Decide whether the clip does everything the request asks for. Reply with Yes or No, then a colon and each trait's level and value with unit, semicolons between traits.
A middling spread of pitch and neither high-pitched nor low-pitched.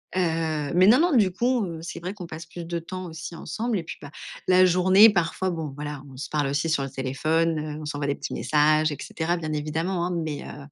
Yes: average, 3.4 semitones; medium, 165 Hz